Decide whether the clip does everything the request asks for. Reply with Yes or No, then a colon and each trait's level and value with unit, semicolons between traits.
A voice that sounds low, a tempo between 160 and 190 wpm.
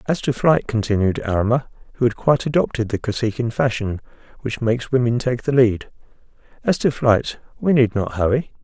Yes: low, 120 Hz; average, 165 wpm